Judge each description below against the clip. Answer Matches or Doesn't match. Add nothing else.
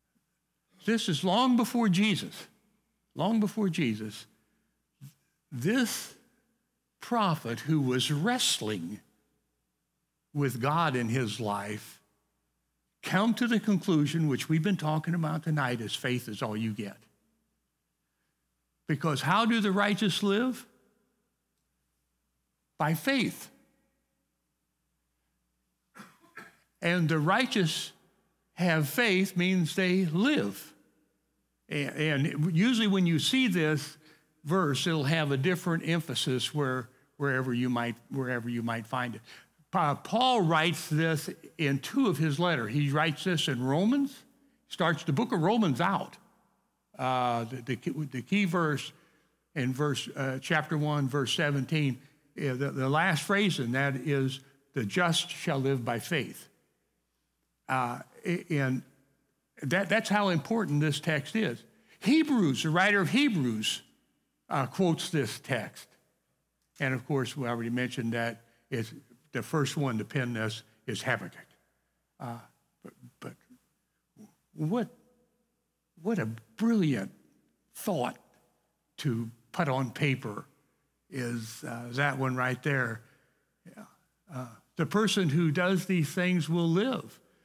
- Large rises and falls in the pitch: Matches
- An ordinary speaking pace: Doesn't match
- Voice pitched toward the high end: Doesn't match